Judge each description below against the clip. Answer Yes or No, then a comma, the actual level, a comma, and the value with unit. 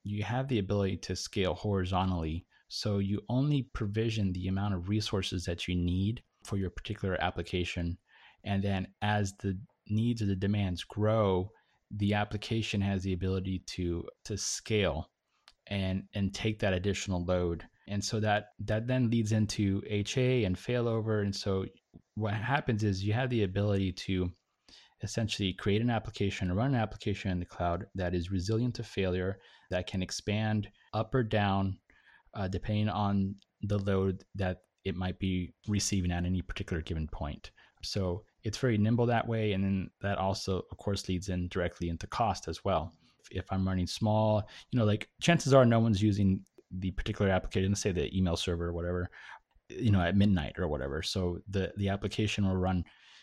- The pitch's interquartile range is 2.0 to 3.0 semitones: Yes, narrow, 2.6 semitones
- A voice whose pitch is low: Yes, low, 100 Hz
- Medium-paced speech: Yes, average, 175 wpm